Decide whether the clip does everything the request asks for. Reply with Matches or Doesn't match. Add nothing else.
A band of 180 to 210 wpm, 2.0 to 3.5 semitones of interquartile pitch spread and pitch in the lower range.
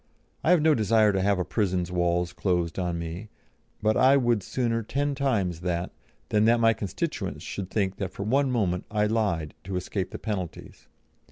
Doesn't match